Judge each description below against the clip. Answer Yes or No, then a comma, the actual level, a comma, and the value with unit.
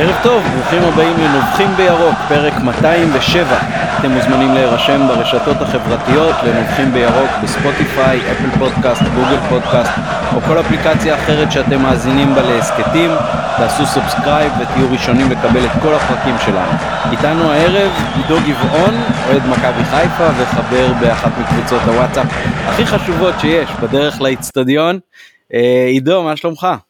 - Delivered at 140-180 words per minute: No, average, 125 wpm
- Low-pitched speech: No, medium, 160 Hz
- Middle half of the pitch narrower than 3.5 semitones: No, average, 4.8 semitones